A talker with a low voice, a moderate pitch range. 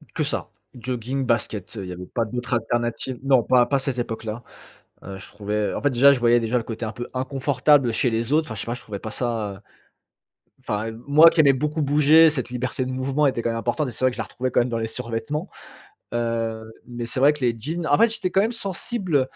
Yes: low, 125 Hz; average, 3.5 semitones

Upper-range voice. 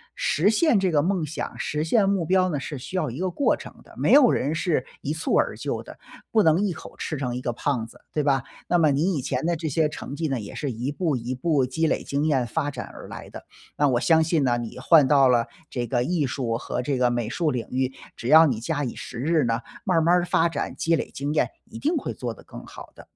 No: medium, 150 Hz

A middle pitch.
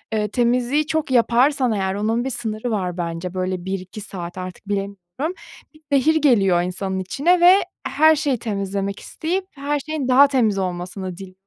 No: high, 215 Hz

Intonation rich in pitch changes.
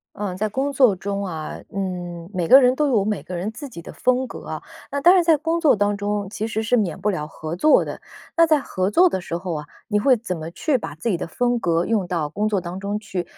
Yes: wide, 5.9 semitones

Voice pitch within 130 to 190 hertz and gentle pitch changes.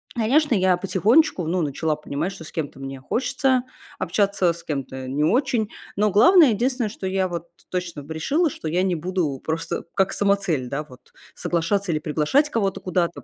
No: medium, 185 Hz; average, 5.3 semitones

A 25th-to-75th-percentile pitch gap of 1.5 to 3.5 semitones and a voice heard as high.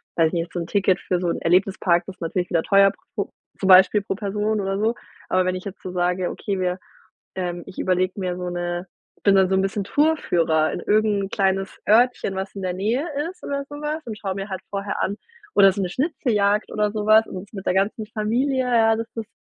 Yes: average, 2.7 semitones; high, 195 Hz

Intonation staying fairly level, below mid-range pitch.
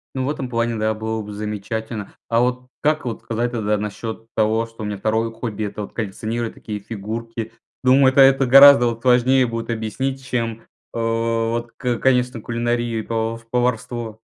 Yes: narrow, 1.9 semitones; low, 115 Hz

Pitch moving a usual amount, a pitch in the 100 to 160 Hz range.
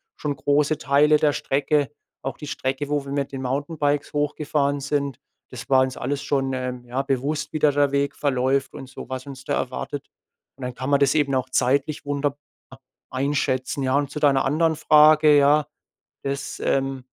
No: narrow, 1.6 semitones; medium, 140 Hz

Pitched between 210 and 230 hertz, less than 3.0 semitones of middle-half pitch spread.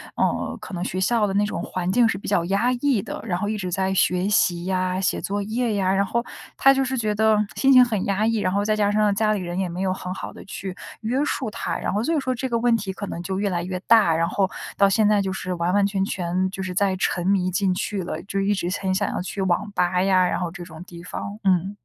No: high, 195 Hz; narrow, 2.5 semitones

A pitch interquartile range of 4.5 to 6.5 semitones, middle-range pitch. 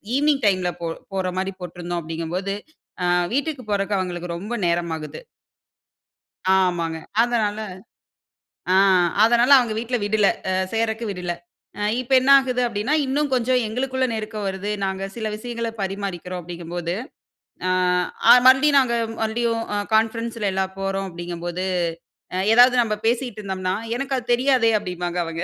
No: average, 4.9 semitones; high, 205 Hz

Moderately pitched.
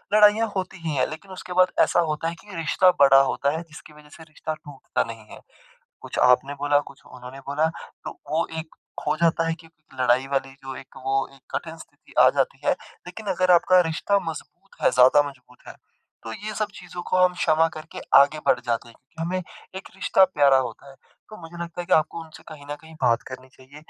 Yes: medium, 155 Hz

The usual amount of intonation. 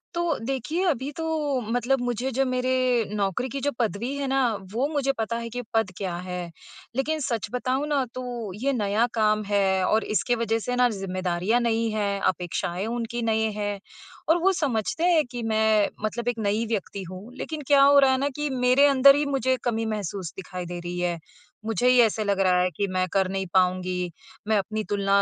Yes: average, 4.7 semitones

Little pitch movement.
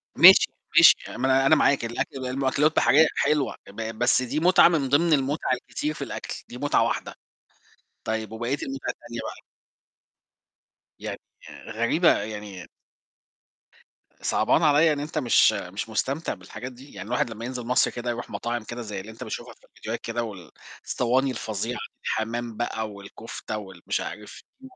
No: average, 3.7 semitones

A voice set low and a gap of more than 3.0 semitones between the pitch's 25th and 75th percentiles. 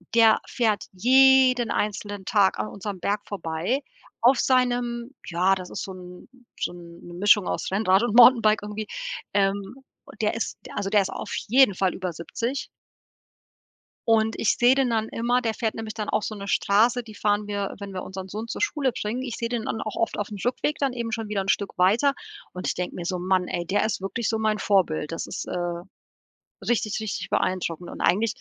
No: high, 210 Hz; average, 3.6 semitones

